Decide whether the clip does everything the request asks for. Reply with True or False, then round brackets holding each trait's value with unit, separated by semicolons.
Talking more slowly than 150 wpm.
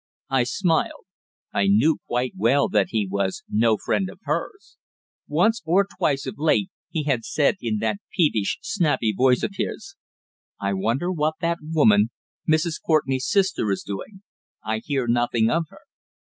False (160 wpm)